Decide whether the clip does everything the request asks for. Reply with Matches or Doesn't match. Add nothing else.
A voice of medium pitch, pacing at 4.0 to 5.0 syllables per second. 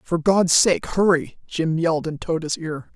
Matches